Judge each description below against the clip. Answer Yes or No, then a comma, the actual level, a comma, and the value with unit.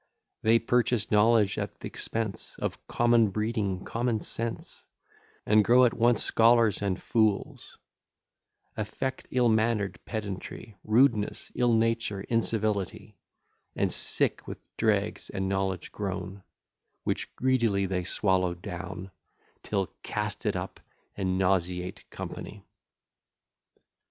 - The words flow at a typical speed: No, slow, 110 wpm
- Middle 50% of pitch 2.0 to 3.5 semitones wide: Yes, average, 3.0 semitones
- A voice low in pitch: Yes, low, 105 Hz